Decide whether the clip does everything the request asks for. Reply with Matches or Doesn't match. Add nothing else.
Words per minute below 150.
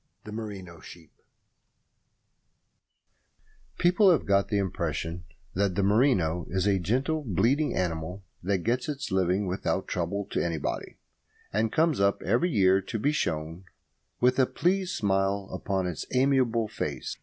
Matches